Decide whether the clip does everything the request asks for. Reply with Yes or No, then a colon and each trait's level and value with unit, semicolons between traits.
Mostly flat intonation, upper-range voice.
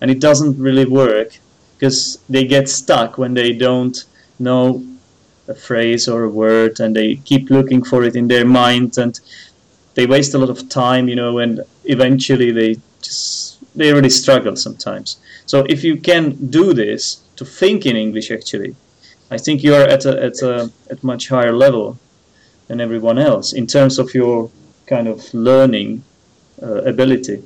No: narrow, 2.3 semitones; low, 125 Hz